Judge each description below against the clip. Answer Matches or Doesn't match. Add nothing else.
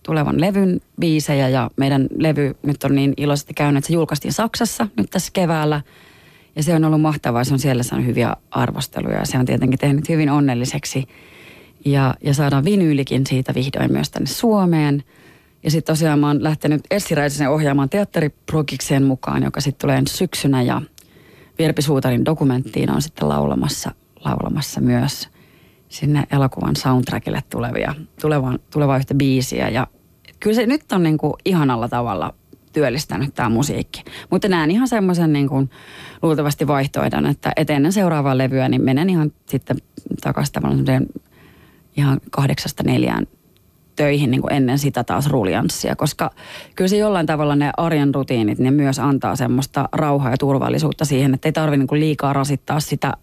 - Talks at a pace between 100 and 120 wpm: Doesn't match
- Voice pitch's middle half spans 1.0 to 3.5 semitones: Matches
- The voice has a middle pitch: Matches